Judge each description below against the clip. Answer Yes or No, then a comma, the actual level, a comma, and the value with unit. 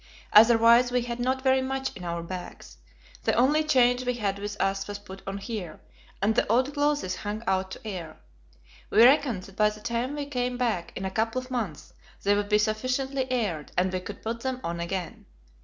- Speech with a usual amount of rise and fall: Yes, average, 4.6 semitones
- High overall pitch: Yes, high, 225 Hz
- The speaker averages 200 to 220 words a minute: Yes, fast, 205 wpm